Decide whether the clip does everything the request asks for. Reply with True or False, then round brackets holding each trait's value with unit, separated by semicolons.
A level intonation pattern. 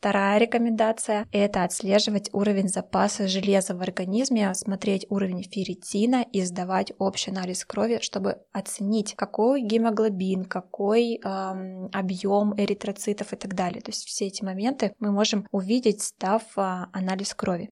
True (2.1 semitones)